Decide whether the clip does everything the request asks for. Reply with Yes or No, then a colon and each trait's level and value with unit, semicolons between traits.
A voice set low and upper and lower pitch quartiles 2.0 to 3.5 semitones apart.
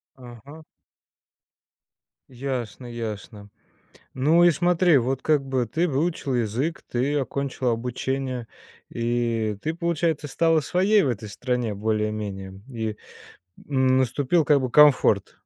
No: low, 130 Hz; average, 4.5 semitones